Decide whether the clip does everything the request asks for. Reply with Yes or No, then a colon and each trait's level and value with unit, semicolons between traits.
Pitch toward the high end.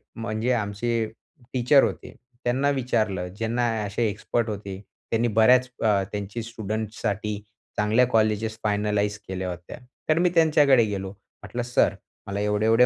No: low, 110 Hz